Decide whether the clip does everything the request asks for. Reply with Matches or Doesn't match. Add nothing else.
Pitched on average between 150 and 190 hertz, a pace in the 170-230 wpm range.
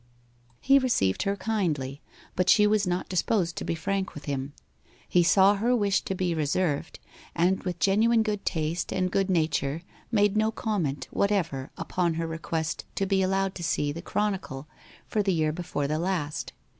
Matches